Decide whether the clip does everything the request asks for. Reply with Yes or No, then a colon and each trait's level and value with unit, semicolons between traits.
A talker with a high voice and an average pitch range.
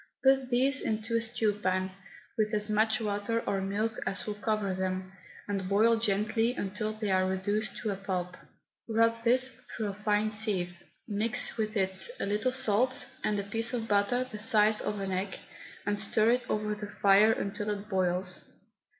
No: high, 210 Hz; narrow, 2.3 semitones